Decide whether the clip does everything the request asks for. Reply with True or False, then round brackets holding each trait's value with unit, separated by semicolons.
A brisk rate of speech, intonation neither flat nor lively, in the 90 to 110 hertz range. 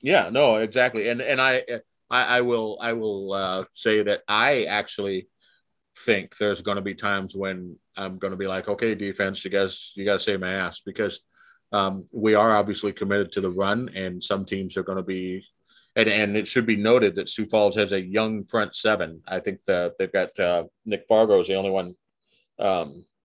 False (210 wpm; 2.3 semitones; 100 Hz)